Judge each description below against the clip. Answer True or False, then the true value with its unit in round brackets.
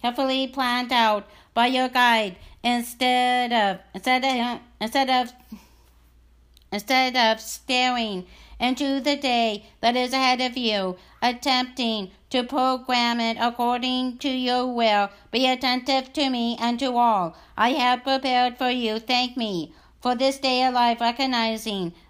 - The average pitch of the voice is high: True (245 Hz)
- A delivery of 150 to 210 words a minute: False (140 wpm)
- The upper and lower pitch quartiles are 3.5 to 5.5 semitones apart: False (2.4 semitones)